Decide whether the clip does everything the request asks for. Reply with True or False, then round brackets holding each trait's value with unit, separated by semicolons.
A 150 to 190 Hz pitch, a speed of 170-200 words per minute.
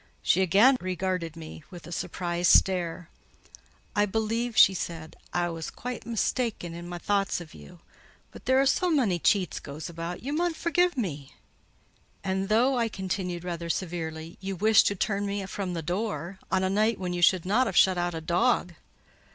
True (185 Hz; 185 wpm)